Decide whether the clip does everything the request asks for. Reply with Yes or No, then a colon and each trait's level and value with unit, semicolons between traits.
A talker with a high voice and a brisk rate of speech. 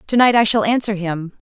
Yes: high, 205 Hz; fast, 245 wpm